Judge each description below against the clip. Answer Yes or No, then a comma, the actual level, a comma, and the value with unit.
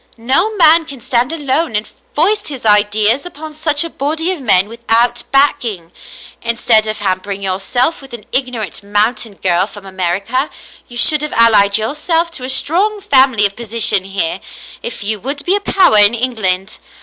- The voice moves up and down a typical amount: No, wide, 5.9 semitones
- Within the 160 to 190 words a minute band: Yes, average, 170 wpm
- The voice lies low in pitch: No, high, 235 Hz